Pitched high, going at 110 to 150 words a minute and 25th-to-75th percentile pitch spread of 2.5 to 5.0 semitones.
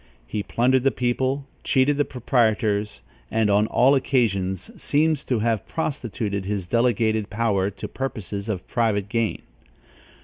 No: low, 115 Hz; slow, 135 wpm; average, 4.2 semitones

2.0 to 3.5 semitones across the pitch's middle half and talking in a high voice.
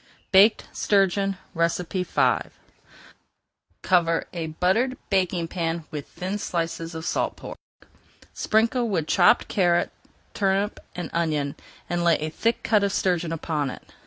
No: average, 3.0 semitones; medium, 175 Hz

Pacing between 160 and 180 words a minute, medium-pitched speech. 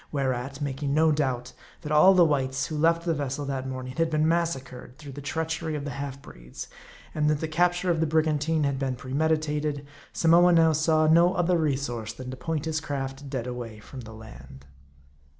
No: average, 195 wpm; medium, 145 Hz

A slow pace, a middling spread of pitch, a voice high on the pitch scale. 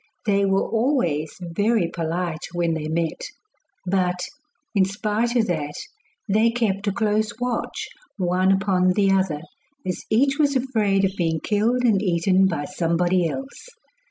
No: average, 145 wpm; average, 4.1 semitones; high, 195 Hz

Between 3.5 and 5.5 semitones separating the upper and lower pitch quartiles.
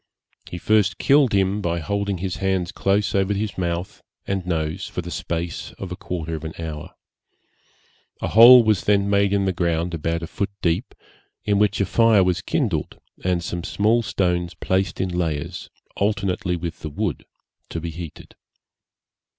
No: average, 2.9 semitones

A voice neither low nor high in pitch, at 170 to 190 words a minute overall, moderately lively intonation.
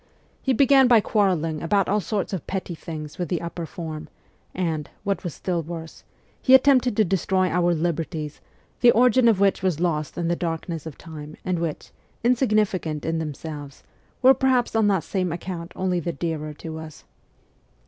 Yes: medium, 175 Hz; average, 175 wpm; average, 4.1 semitones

